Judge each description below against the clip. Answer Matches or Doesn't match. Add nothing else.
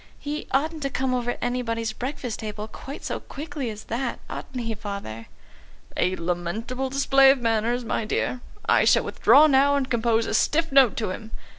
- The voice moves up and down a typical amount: Matches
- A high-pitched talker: Matches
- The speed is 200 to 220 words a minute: Doesn't match